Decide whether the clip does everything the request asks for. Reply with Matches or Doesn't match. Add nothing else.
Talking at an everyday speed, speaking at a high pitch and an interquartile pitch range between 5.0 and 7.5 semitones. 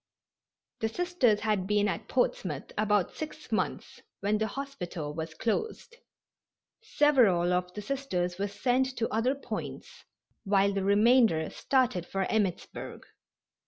Doesn't match